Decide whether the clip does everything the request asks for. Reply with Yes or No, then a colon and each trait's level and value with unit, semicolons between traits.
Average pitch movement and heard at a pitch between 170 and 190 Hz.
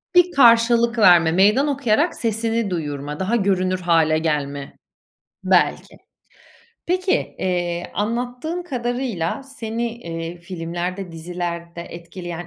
No: wide, 5.8 semitones; medium, 185 Hz